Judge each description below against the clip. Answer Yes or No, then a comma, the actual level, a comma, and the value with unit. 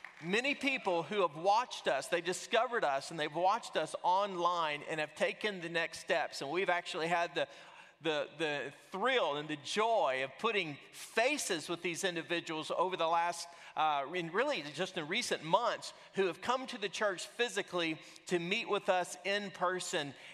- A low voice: No, medium, 180 Hz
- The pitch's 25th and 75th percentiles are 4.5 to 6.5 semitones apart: No, average, 3.3 semitones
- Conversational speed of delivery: Yes, average, 175 wpm